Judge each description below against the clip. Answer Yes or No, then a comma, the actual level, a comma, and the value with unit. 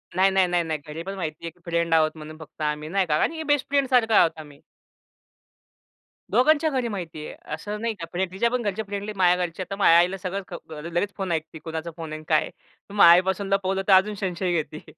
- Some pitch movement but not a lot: Yes, average, 3.9 semitones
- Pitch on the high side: No, medium, 180 Hz